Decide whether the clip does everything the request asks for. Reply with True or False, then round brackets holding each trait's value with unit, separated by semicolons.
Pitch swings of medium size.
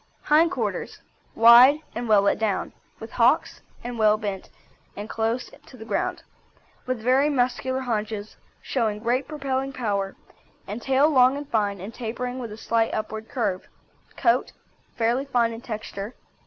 True (3.1 semitones)